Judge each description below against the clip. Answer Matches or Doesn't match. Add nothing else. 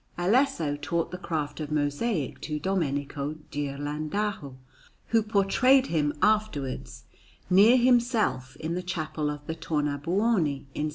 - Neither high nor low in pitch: Matches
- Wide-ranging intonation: Matches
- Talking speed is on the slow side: Matches